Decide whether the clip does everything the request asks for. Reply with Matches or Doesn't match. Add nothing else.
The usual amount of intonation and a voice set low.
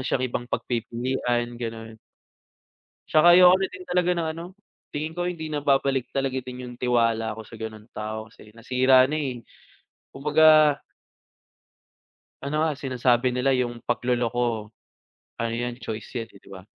Matches